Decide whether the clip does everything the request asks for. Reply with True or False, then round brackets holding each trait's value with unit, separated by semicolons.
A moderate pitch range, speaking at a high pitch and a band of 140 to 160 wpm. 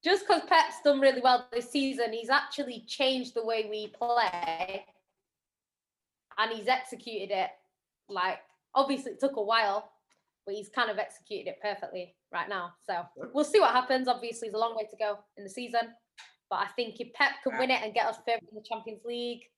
False (3.4 semitones; 235 Hz; 200 wpm)